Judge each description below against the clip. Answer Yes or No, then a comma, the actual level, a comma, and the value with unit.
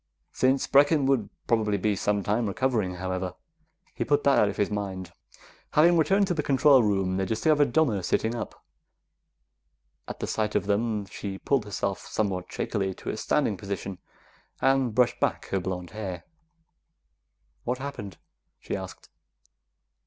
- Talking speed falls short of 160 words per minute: Yes, average, 150 wpm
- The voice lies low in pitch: Yes, low, 105 Hz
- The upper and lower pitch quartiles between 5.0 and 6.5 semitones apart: Yes, wide, 5.5 semitones